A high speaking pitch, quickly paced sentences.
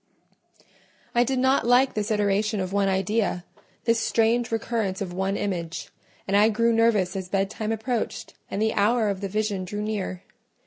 No: high, 210 Hz; average, 165 wpm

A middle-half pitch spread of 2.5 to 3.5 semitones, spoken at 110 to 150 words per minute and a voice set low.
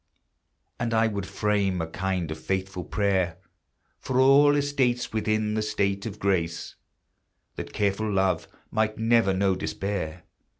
Yes: average, 2.8 semitones; slow, 135 wpm; low, 100 Hz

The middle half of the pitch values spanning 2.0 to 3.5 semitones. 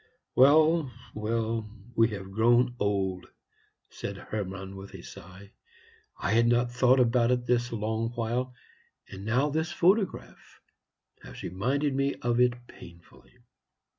Yes: average, 3.1 semitones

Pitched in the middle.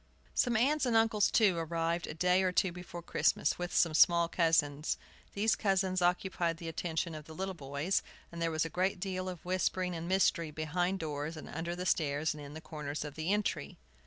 Yes: medium, 170 Hz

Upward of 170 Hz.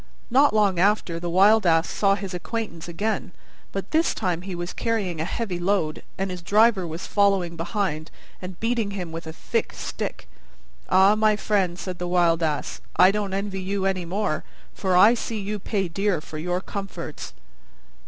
Yes: high, 190 Hz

